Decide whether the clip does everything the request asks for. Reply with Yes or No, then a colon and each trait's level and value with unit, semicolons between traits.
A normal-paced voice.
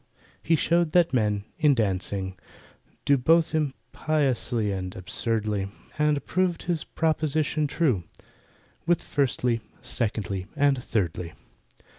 No: slow, 105 wpm